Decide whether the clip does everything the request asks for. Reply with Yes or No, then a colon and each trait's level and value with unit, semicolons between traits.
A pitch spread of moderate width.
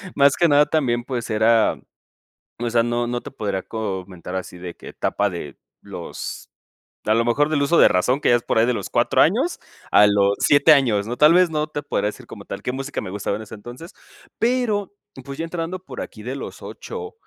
No: wide, 6.0 semitones